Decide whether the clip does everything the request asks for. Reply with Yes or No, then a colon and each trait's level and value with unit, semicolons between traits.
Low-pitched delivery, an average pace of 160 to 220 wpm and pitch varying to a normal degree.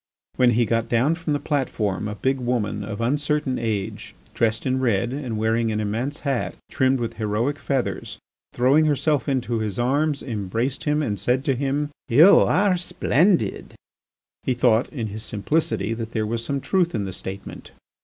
Yes: low, 120 Hz; average, 175 wpm; average, 4.5 semitones